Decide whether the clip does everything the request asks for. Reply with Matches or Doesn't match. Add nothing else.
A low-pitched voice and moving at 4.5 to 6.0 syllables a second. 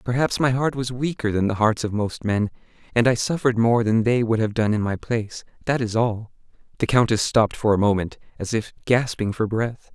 Matches